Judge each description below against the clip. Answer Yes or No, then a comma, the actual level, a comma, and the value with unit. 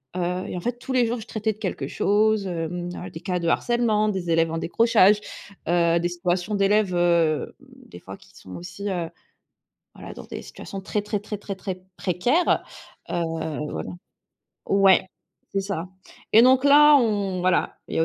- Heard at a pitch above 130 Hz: Yes, high, 190 Hz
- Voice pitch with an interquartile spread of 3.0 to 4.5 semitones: Yes, average, 3.6 semitones